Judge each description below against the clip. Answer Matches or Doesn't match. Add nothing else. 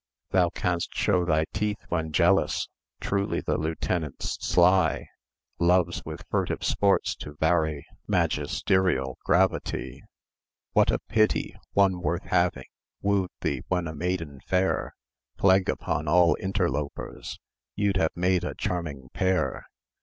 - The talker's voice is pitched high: Doesn't match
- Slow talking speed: Matches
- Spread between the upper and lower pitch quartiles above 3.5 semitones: Doesn't match